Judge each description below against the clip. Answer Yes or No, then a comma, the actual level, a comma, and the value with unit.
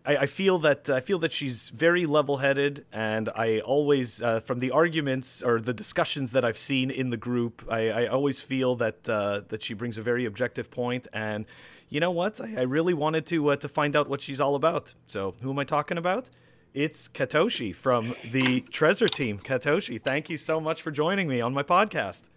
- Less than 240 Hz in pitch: Yes, low, 135 Hz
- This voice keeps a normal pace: No, fast, 210 wpm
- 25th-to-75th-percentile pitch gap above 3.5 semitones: Yes, average, 4.1 semitones